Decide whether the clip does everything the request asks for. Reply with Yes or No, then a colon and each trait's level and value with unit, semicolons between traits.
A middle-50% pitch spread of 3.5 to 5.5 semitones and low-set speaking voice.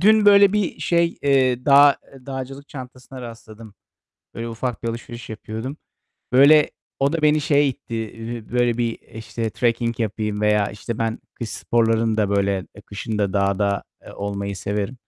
Yes: average, 4.1 semitones; low, 115 Hz